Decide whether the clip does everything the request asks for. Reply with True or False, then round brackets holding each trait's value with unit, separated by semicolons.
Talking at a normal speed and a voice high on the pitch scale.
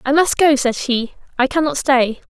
False (210 wpm; 275 Hz)